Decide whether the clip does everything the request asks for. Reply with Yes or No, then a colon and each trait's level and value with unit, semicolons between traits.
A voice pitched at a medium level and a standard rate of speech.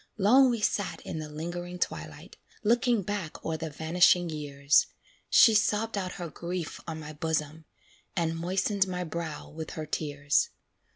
Yes: medium, 170 Hz; average, 155 wpm